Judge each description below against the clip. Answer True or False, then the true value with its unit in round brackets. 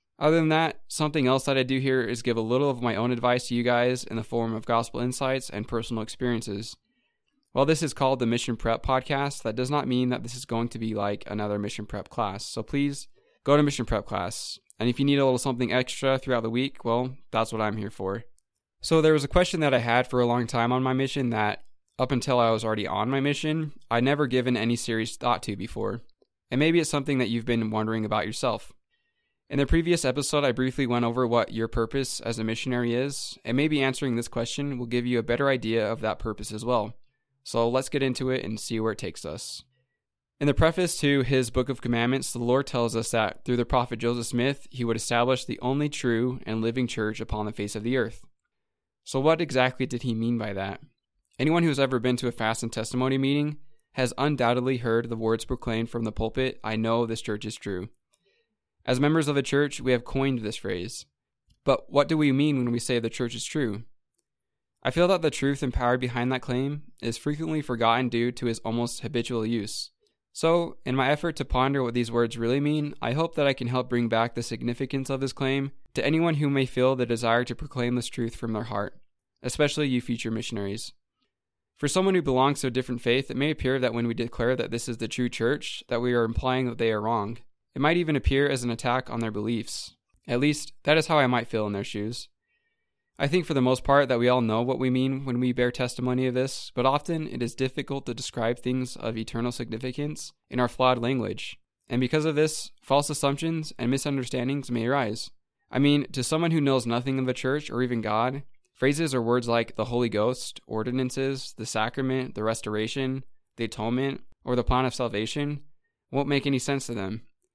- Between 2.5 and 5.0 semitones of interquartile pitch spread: True (3.0 semitones)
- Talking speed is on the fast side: True (225 wpm)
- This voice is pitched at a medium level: False (125 Hz)